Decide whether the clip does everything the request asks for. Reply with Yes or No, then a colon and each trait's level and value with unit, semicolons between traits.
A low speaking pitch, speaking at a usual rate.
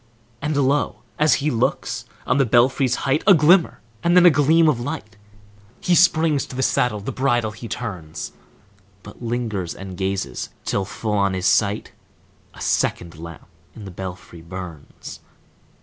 Yes: low, 115 Hz; average, 160 wpm